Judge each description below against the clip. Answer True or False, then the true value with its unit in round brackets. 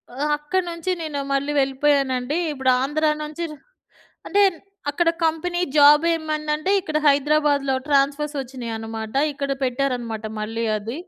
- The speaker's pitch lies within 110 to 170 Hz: False (285 Hz)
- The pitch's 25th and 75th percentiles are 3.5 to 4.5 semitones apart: False (2.7 semitones)